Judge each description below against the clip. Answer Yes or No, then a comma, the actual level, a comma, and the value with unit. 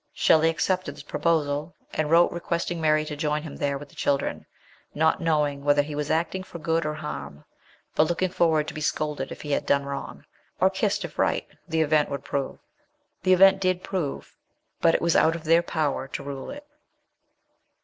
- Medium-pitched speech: Yes, medium, 155 Hz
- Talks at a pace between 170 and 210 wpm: Yes, average, 195 wpm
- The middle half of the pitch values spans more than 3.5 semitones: No, average, 2.7 semitones